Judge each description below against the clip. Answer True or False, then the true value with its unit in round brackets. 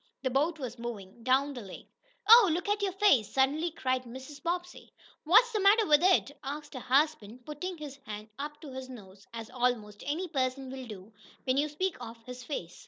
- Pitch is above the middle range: True (270 Hz)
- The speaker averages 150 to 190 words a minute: False (200 wpm)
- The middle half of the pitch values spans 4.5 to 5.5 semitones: True (5.0 semitones)